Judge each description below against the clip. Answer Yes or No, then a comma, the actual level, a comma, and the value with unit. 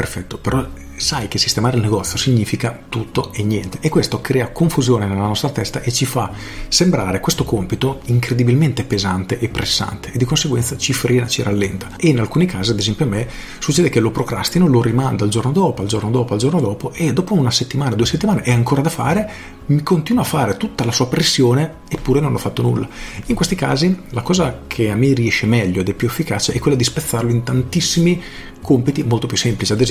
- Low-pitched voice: Yes, low, 125 Hz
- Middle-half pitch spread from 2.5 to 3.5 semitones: No, average, 4.8 semitones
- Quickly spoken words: Yes, fast, 215 wpm